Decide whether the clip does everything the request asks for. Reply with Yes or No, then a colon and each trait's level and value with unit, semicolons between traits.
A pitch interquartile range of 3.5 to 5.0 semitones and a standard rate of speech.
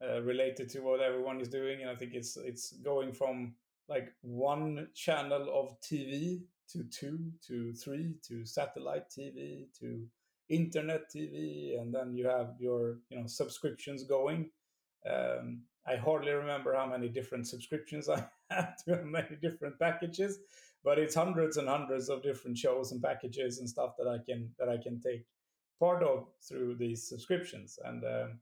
Yes: average, 4.0 semitones; average, 165 wpm